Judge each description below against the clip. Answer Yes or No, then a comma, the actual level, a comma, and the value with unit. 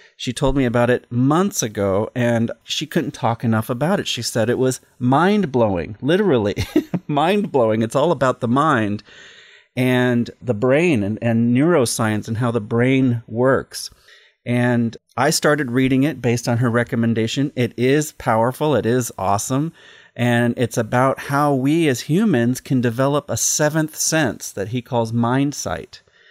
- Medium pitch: No, low, 125 Hz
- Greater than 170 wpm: No, average, 160 wpm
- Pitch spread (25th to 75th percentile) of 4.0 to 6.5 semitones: No, average, 3.4 semitones